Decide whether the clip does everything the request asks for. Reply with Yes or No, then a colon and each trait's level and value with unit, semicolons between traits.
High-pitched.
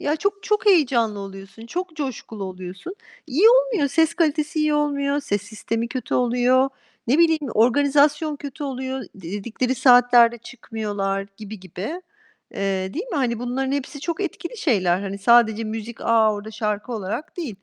Yes: high, 245 Hz